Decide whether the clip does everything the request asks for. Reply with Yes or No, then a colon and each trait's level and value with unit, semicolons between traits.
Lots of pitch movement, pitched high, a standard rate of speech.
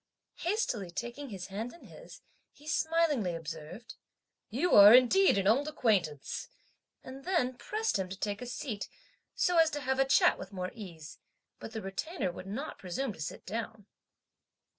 Yes: wide, 7.1 semitones; high, 230 Hz; average, 165 wpm